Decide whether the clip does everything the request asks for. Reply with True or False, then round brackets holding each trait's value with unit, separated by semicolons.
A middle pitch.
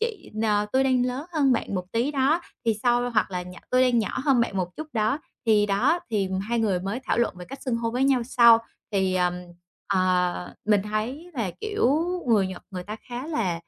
False (235 Hz)